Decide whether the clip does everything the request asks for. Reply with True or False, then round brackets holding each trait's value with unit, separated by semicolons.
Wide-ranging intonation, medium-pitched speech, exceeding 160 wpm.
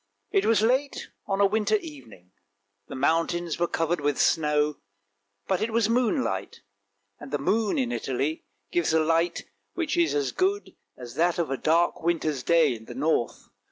True (6.5 semitones; 165 Hz; 170 wpm)